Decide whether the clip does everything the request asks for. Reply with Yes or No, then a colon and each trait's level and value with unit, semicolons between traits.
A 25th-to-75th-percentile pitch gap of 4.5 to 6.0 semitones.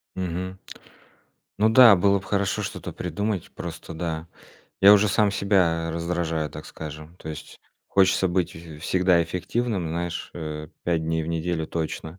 No: average, 2.9 semitones